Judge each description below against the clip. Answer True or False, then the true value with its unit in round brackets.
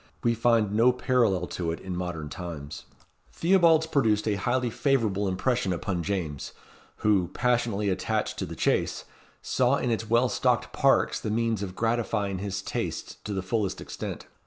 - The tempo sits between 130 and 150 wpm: False (160 wpm)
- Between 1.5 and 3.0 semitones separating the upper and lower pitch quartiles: False (4.3 semitones)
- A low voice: True (105 Hz)